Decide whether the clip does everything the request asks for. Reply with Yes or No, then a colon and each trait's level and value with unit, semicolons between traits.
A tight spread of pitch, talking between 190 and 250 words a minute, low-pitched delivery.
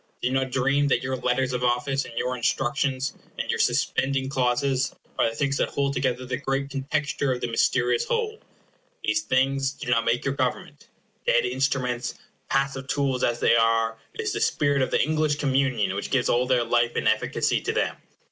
Yes: narrow, 2.0 semitones; average, 195 wpm; low, 130 Hz